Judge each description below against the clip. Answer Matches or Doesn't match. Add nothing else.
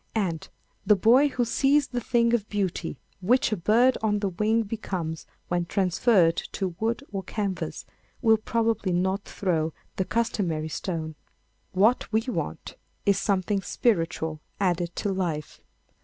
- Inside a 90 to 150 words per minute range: Matches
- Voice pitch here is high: Matches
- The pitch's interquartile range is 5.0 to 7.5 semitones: Doesn't match